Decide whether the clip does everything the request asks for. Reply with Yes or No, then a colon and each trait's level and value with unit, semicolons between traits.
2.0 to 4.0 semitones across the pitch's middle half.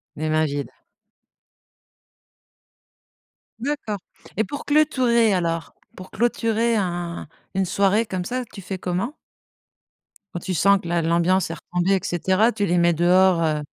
No: average, 4.4 semitones